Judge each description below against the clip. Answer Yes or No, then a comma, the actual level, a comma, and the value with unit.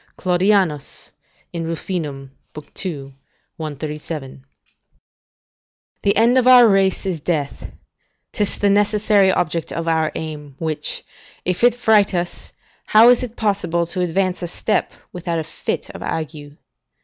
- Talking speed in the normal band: No, slow, 130 wpm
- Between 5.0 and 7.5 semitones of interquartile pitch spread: No, average, 4.5 semitones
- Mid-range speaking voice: Yes, medium, 175 Hz